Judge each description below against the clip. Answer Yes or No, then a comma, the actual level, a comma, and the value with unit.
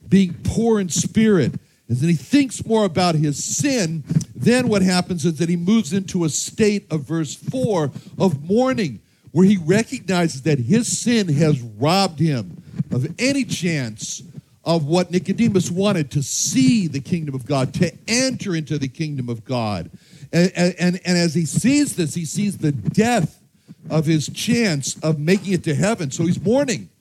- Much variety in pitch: No, average, 4.5 semitones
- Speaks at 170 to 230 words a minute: Yes, average, 175 wpm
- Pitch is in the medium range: Yes, medium, 175 Hz